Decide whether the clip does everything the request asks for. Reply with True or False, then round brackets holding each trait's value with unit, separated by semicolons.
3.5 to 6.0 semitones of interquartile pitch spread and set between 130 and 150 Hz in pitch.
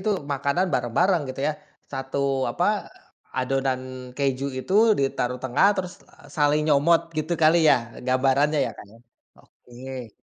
False (3.0 semitones; 140 Hz)